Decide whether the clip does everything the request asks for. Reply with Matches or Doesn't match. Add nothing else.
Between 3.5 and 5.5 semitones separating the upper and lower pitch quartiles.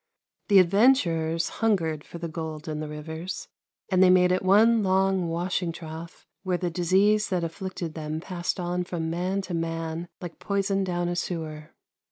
Doesn't match